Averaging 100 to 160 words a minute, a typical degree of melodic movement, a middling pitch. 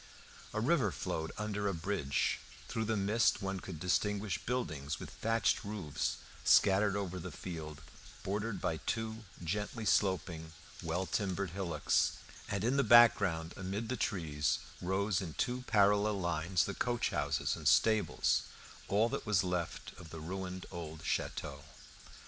No: average, 145 wpm; average, 4.0 semitones; very low, 95 Hz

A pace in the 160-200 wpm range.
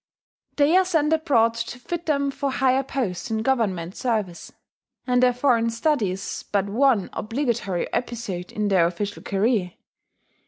No: average, 150 wpm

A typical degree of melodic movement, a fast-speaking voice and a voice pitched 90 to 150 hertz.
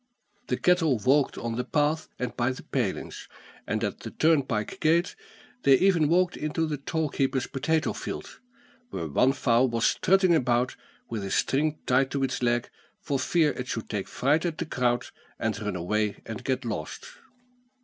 No: average, 4.7 semitones; average, 175 wpm; low, 135 Hz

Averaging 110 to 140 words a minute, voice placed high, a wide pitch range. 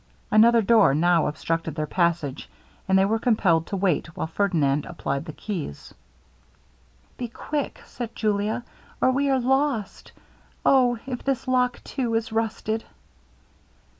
Yes: slow, 135 wpm; high, 215 Hz; wide, 6.4 semitones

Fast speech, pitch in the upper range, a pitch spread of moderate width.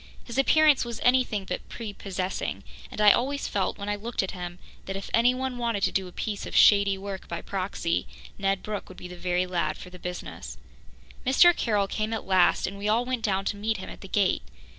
Yes: fast, 220 wpm; high, 200 Hz; average, 3.6 semitones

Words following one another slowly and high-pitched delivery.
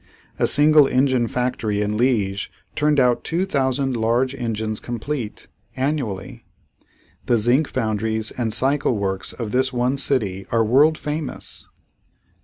No: slow, 130 wpm; low, 125 Hz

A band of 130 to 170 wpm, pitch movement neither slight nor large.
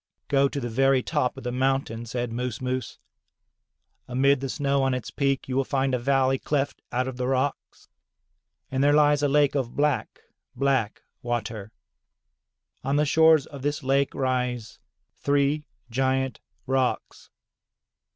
No: average, 150 wpm; narrow, 1.8 semitones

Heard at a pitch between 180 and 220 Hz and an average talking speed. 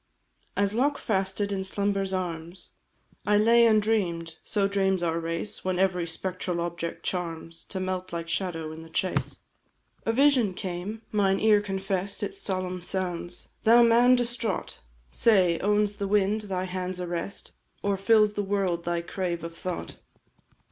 Yes: high, 190 Hz; average, 150 wpm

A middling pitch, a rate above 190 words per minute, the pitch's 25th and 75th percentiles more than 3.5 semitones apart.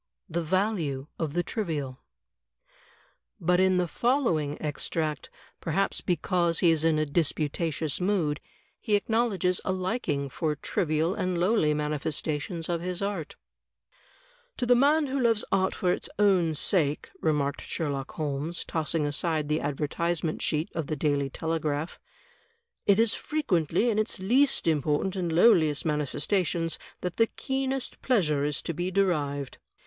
No: medium, 165 Hz; average, 145 wpm; average, 4.3 semitones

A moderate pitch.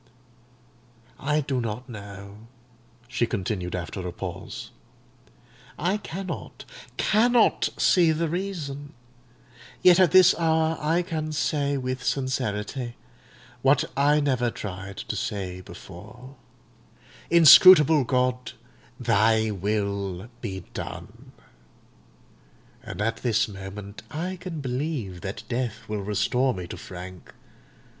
No: low, 125 Hz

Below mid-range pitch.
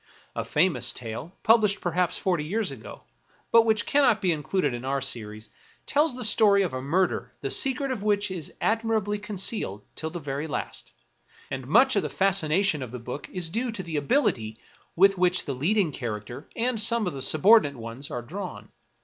No: medium, 180 Hz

